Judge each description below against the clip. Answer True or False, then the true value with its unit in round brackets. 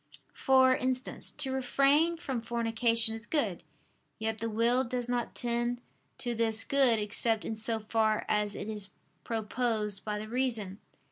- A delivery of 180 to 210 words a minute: False (150 wpm)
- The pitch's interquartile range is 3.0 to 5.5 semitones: False (2.5 semitones)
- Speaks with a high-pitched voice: True (230 Hz)